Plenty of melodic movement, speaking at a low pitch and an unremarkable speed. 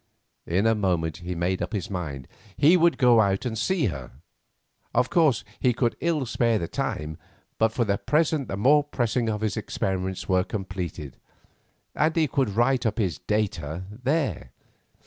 Yes: wide, 5.9 semitones; low, 110 Hz; average, 170 wpm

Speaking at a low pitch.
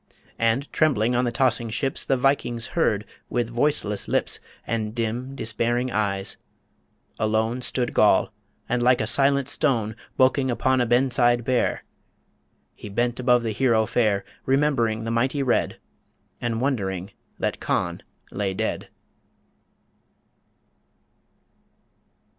Yes: low, 120 Hz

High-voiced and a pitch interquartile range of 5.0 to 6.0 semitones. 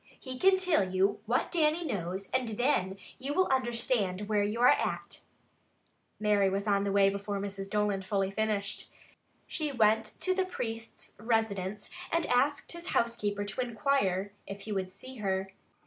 No: high, 210 Hz; average, 4.4 semitones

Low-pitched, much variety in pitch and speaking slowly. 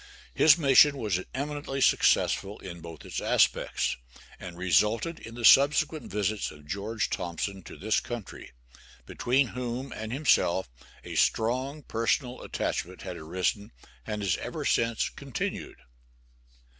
Yes: low, 110 Hz; wide, 6.2 semitones; slow, 130 wpm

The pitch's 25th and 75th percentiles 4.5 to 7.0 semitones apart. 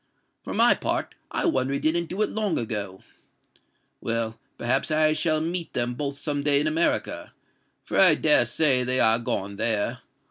Yes: average, 5.1 semitones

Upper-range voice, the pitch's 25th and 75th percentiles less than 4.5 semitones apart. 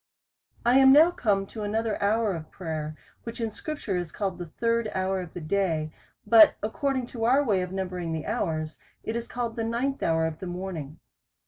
No: high, 200 Hz; average, 5.1 semitones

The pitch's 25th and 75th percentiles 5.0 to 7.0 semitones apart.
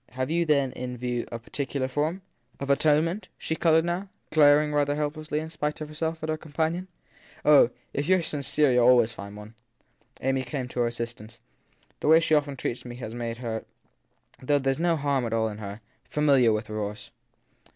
No: average, 4.4 semitones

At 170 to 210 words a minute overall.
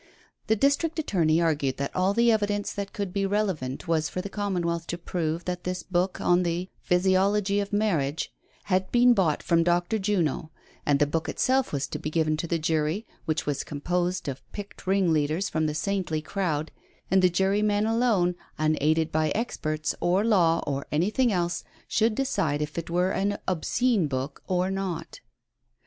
Yes: average, 175 wpm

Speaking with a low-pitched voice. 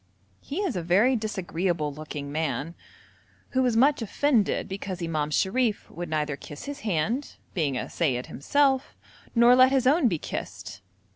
No: high, 195 Hz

